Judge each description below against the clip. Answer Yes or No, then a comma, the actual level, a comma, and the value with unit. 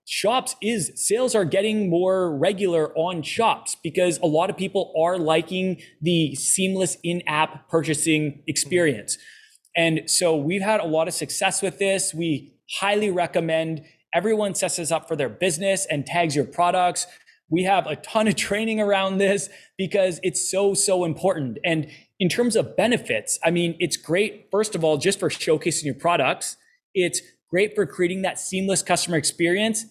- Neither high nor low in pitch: Yes, medium, 180 Hz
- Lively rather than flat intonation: No, average, 3.2 semitones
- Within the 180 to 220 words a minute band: No, average, 165 wpm